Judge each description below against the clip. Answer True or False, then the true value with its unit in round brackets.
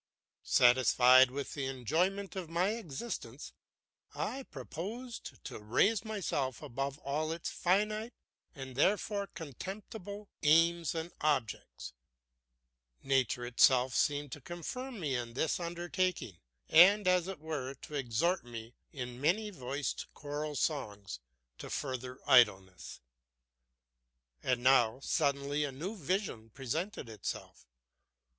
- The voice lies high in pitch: False (145 Hz)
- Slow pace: True (115 wpm)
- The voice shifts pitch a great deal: True (6.2 semitones)